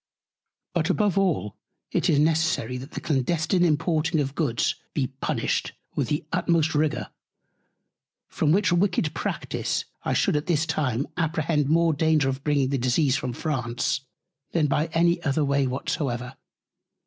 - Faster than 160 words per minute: No, average, 150 wpm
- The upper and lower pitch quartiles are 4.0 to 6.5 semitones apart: No, average, 3.3 semitones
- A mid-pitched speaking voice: Yes, medium, 150 Hz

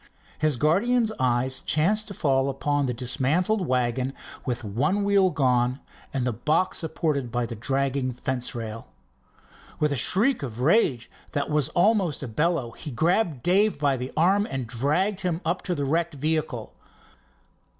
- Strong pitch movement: Yes, wide, 5.8 semitones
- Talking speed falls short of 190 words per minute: Yes, average, 160 wpm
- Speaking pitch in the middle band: Yes, medium, 145 Hz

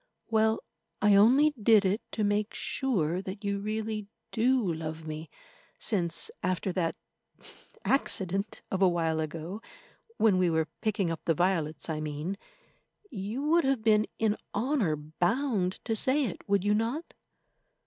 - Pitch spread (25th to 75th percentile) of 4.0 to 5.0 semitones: Yes, average, 4.6 semitones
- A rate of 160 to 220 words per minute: No, average, 145 wpm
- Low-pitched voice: No, high, 200 Hz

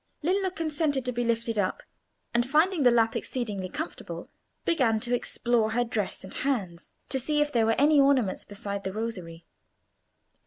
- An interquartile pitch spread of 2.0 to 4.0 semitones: No, average, 4.6 semitones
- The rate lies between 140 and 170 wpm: Yes, average, 165 wpm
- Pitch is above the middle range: Yes, high, 240 Hz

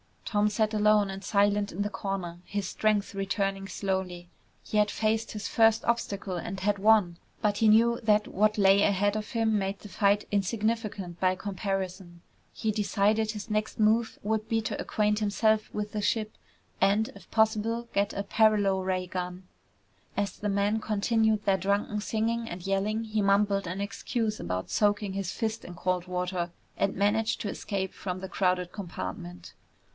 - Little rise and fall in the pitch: Yes, narrow, 2.0 semitones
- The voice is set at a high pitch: Yes, high, 205 Hz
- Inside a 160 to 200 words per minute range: Yes, average, 170 wpm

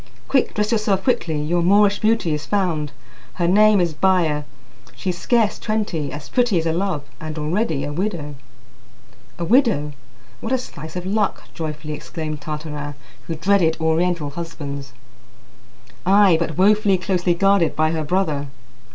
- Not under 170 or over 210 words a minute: No, average, 150 wpm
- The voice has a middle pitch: Yes, medium, 170 Hz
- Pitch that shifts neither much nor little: Yes, average, 4.6 semitones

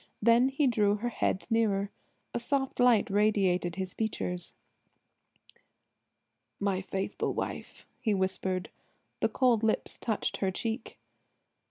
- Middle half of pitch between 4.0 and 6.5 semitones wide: No, average, 3.6 semitones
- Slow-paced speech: Yes, slow, 120 wpm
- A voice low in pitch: No, high, 210 Hz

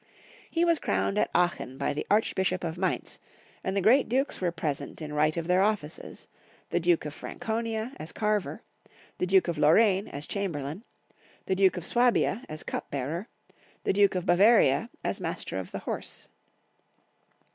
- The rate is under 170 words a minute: No, average, 175 wpm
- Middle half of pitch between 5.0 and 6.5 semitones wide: Yes, wide, 5.4 semitones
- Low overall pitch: No, medium, 185 Hz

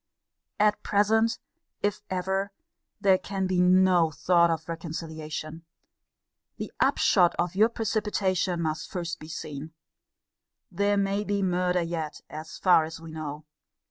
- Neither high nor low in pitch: Yes, medium, 180 Hz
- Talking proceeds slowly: Yes, slow, 130 wpm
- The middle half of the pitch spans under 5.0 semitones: Yes, average, 3.5 semitones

